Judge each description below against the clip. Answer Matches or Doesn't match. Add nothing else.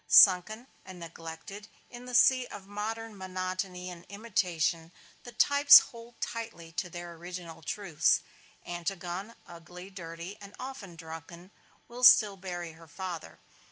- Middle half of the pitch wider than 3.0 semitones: Matches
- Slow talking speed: Matches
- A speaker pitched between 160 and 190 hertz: Matches